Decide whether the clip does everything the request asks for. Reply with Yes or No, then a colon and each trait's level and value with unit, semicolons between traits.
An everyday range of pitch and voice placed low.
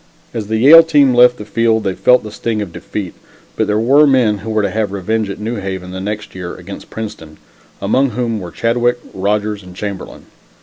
Yes: average, 3.0 semitones; low, 105 Hz